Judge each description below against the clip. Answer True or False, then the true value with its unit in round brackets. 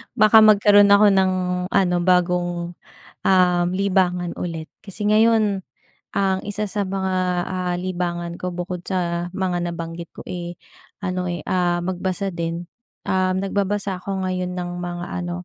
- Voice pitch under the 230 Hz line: True (185 Hz)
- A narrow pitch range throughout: True (1.8 semitones)